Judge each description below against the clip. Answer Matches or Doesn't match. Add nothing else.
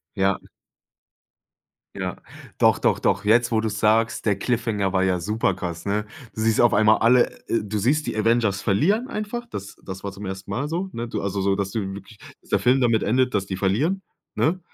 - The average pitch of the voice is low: Matches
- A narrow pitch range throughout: Doesn't match